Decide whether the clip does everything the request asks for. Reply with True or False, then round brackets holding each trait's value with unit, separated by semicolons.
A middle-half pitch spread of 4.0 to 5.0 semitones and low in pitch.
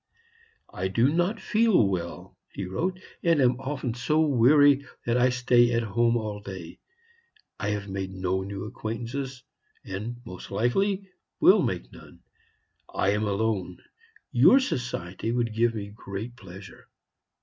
True (4.7 semitones; 115 Hz)